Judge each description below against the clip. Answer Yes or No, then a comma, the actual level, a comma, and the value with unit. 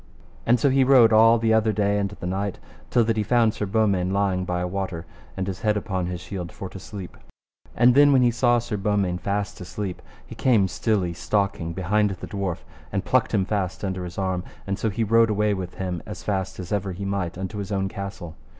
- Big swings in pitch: No, average, 2.7 semitones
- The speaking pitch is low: Yes, low, 100 Hz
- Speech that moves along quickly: Yes, fast, 225 wpm